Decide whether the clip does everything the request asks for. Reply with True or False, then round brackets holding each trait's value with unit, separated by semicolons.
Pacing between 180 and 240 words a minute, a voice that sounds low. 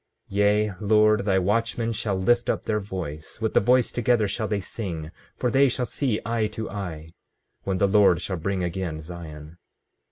True (185 wpm; 100 Hz)